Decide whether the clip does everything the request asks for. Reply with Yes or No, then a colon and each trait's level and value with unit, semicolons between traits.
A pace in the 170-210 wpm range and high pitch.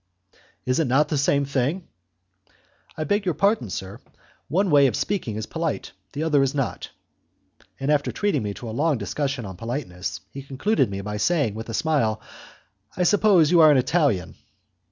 No: average, 175 wpm; medium, 140 Hz